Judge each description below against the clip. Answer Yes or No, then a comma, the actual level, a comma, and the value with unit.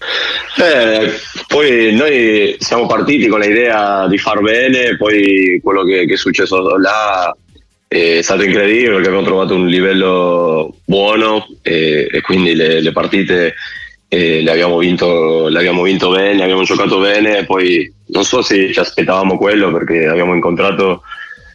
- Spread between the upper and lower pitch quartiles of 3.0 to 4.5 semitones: Yes, average, 3.6 semitones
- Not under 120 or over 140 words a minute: No, average, 150 wpm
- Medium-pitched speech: No, very low, 95 Hz